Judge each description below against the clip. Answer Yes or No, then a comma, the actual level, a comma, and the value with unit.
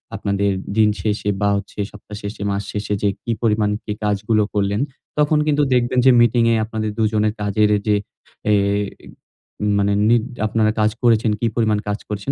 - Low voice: Yes, low, 105 Hz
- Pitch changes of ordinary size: No, narrow, 1.9 semitones